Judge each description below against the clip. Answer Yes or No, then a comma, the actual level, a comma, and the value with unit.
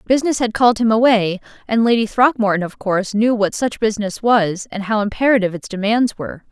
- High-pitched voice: Yes, high, 215 Hz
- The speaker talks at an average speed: Yes, average, 195 wpm